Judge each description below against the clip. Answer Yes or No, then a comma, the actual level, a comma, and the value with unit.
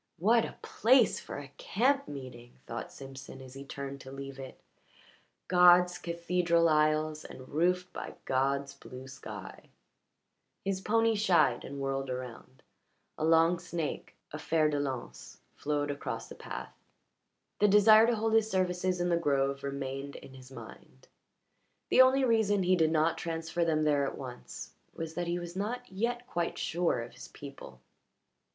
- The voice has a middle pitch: Yes, medium, 160 Hz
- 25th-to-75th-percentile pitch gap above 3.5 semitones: Yes, average, 5.1 semitones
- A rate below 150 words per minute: No, average, 160 wpm